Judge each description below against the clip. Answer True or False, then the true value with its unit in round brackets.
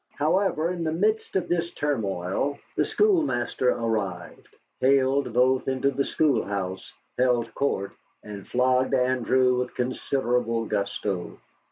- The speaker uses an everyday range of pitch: True (4.0 semitones)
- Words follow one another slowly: True (120 wpm)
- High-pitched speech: False (125 Hz)